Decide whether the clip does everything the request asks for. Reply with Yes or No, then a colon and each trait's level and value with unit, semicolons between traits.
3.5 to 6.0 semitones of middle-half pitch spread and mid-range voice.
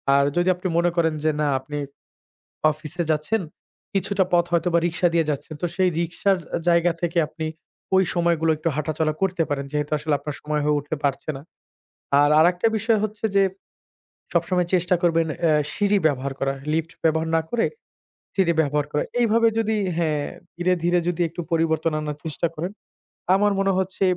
No: average, 3.1 semitones; medium, 170 Hz